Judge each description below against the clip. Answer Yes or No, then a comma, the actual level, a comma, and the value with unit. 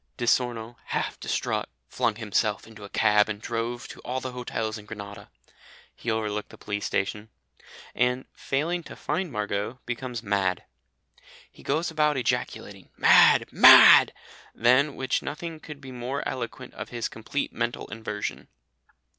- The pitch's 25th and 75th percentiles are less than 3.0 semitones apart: No, average, 3.6 semitones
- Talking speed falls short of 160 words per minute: Yes, average, 145 wpm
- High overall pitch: No, low, 120 Hz